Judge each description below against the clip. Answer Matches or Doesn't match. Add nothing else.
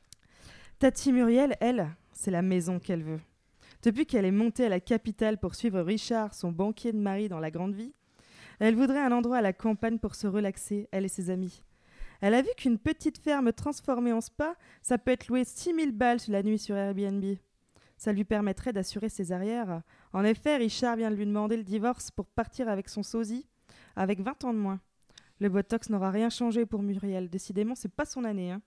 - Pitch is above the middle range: Matches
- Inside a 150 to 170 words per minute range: Doesn't match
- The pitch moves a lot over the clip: Doesn't match